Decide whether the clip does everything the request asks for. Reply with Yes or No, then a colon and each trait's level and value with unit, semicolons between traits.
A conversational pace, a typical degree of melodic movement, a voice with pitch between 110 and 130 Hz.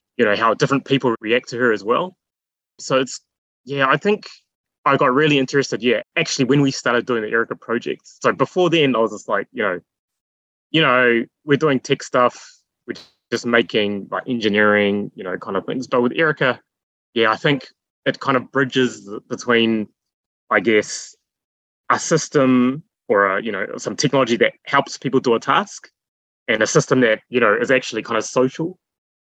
Yes: average, 185 wpm; average, 3.8 semitones; low, 125 Hz